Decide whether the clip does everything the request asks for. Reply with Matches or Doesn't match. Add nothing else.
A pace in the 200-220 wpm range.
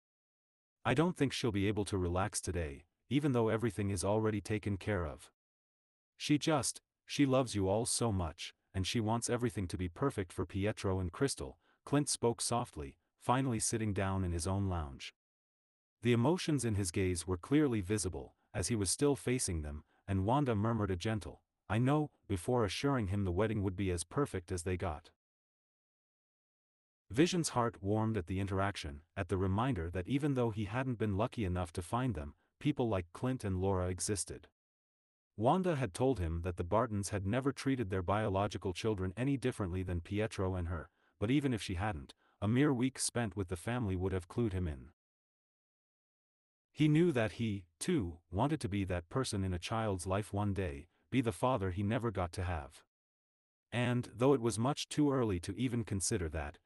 Doesn't match